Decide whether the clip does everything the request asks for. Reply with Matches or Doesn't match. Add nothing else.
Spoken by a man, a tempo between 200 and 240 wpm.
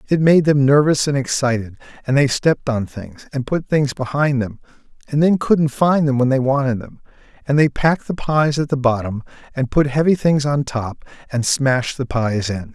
Matches